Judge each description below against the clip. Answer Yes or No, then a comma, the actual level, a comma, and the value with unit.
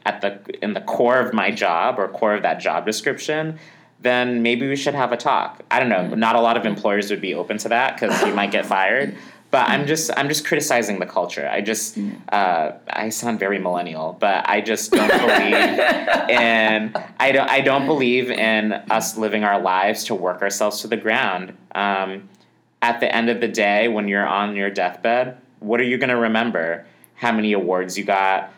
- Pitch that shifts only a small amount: No, average, 3.8 semitones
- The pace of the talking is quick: Yes, fast, 210 wpm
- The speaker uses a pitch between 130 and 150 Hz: No, low, 110 Hz